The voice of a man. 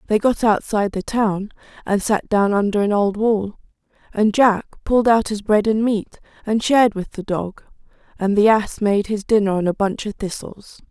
No: female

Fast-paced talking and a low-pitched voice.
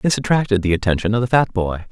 Yes: fast, 250 wpm; low, 110 Hz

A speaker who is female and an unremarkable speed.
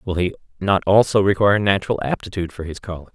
No: male; average, 190 wpm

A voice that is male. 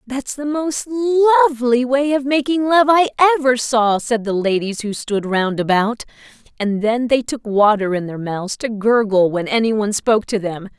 No: female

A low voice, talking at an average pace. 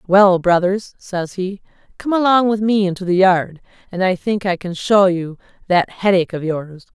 No: high, 190 Hz; average, 190 wpm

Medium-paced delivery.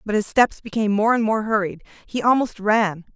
No: fast, 210 wpm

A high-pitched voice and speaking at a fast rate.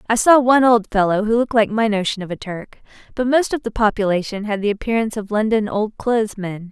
Yes: high, 215 Hz; fast, 230 wpm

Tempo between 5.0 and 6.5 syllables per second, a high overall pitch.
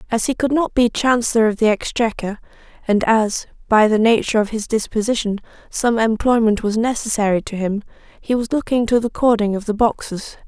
Yes: 5.5 syllables/s; high, 225 Hz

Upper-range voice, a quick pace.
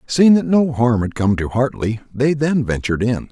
No: low, 125 Hz; fast, 215 wpm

